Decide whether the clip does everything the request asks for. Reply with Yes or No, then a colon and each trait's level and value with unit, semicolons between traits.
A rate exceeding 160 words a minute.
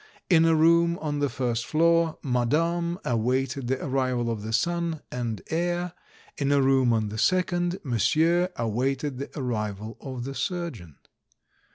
No: average, 150 wpm